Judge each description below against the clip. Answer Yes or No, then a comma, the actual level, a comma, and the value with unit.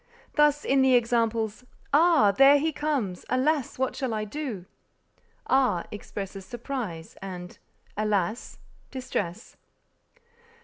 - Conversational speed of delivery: No, slow, 105 wpm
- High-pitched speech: Yes, high, 240 Hz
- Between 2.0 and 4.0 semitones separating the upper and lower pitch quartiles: No, average, 5.2 semitones